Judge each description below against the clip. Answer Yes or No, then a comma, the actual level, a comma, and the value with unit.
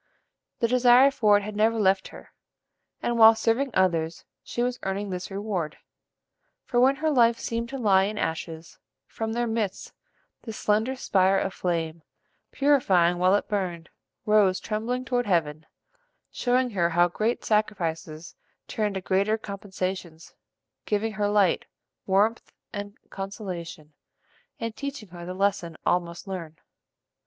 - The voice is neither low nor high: No, high, 205 Hz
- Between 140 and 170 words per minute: Yes, average, 145 wpm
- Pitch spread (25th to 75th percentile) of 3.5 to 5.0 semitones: Yes, average, 4.1 semitones